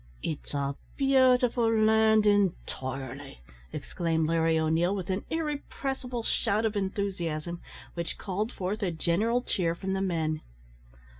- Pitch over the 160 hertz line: Yes, high, 190 Hz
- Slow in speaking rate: Yes, slow, 125 wpm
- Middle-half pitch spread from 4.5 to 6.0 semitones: Yes, average, 5.1 semitones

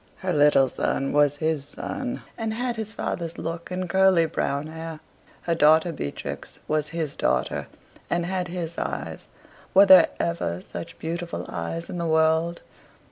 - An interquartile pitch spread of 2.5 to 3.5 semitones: Yes, average, 2.9 semitones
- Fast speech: No, average, 155 wpm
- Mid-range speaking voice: Yes, medium, 165 Hz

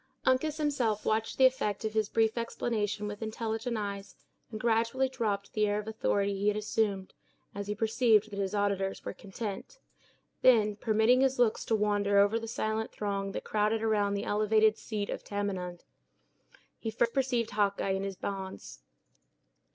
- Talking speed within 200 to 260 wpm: No, average, 165 wpm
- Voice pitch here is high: Yes, high, 215 Hz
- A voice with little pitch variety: Yes, narrow, 2.0 semitones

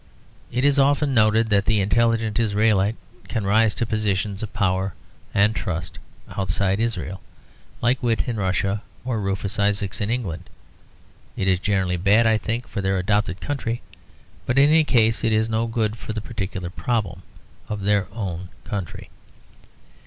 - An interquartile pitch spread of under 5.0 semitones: Yes, average, 2.9 semitones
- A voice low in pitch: Yes, low, 105 Hz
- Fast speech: No, average, 160 wpm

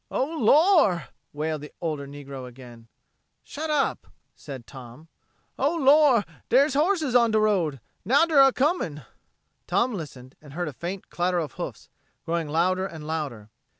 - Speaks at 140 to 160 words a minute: Yes, average, 150 wpm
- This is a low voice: No, medium, 175 Hz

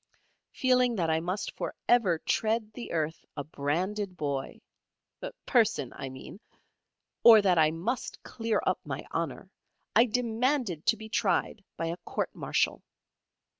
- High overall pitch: Yes, high, 200 Hz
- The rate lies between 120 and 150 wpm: Yes, average, 140 wpm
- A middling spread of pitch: No, wide, 6.1 semitones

